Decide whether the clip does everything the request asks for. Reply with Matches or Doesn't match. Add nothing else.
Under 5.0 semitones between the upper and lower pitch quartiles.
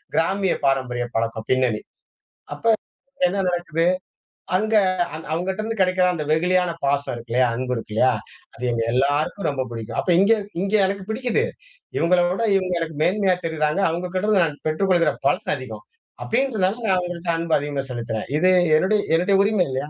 Doesn't match